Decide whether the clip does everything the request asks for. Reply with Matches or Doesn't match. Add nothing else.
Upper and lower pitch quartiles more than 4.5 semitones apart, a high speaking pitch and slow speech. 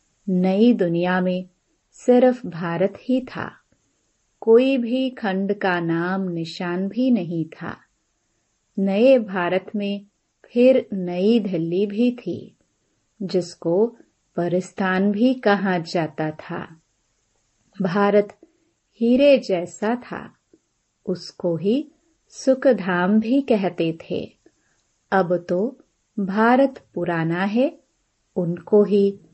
Matches